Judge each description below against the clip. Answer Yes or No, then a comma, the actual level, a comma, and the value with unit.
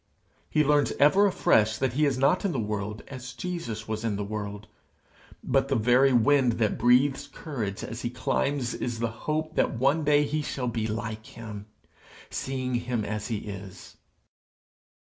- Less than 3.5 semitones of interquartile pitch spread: No, average, 4.5 semitones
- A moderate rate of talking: Yes, average, 170 wpm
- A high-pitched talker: No, low, 120 Hz